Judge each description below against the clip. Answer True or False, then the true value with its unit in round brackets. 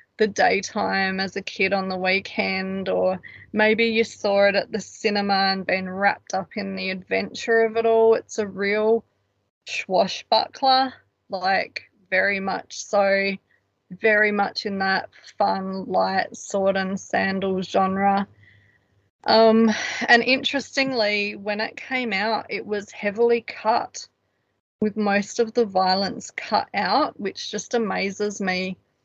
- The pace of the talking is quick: False (135 wpm)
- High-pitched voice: True (200 Hz)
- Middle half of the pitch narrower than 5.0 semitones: True (2.4 semitones)